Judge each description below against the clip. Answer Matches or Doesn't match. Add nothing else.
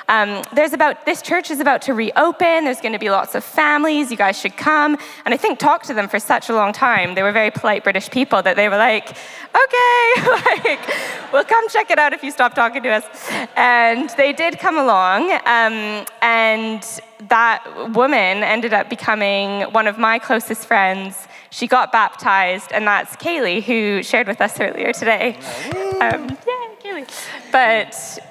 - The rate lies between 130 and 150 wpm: Doesn't match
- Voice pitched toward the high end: Matches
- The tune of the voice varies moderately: Doesn't match